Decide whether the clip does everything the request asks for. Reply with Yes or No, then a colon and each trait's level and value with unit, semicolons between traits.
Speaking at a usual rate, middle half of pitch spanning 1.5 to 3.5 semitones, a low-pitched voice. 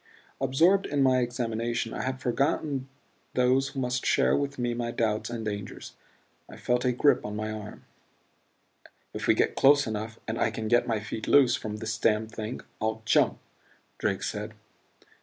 Yes: average, 175 wpm; average, 3.0 semitones; low, 120 Hz